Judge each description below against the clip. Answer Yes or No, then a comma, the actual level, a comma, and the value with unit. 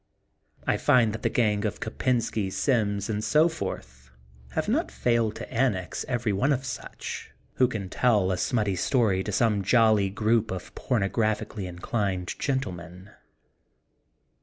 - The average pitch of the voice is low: Yes, low, 105 Hz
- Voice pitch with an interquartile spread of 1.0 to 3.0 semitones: No, average, 3.8 semitones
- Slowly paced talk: No, average, 145 wpm